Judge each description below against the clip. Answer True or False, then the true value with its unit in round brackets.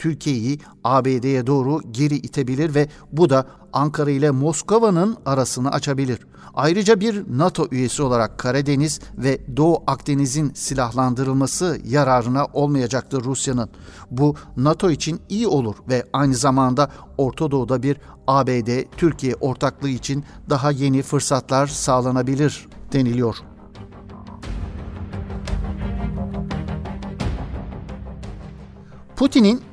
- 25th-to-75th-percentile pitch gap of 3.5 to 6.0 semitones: False (2.7 semitones)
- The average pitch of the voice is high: False (135 Hz)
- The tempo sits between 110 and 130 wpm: False (95 wpm)